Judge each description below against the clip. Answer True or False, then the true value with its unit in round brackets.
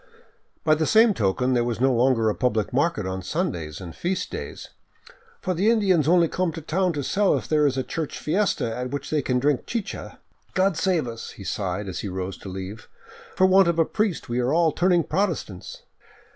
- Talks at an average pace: False (220 wpm)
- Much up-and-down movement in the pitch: True (8.0 semitones)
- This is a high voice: False (150 Hz)